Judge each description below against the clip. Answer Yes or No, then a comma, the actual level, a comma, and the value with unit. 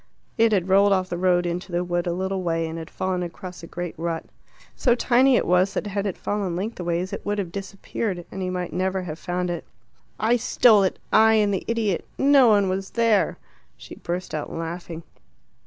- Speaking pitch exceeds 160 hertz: Yes, medium, 185 Hz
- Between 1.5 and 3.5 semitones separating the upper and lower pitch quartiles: Yes, average, 2.8 semitones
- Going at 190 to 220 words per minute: Yes, fast, 205 wpm